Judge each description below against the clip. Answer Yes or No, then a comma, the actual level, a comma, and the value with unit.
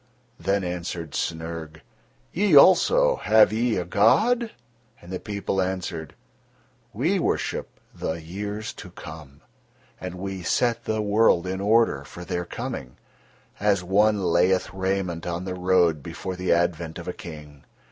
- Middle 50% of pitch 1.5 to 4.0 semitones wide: Yes, average, 3.4 semitones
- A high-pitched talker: No, very low, 90 Hz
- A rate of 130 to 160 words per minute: Yes, average, 140 wpm